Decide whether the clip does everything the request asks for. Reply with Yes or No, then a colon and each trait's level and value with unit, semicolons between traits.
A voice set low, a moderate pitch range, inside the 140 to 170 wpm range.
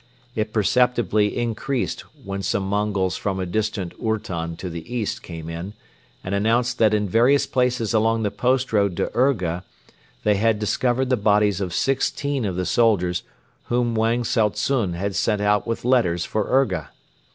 Yes: low, 105 Hz; average, 3.8 semitones; average, 165 wpm